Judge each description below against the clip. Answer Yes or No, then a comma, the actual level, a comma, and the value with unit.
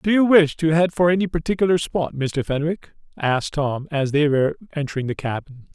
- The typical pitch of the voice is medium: Yes, medium, 155 Hz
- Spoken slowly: No, average, 200 wpm